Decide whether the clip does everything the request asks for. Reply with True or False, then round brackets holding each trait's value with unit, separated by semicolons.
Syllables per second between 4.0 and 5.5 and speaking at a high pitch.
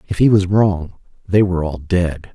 False (5.0 syllables/s; 90 Hz)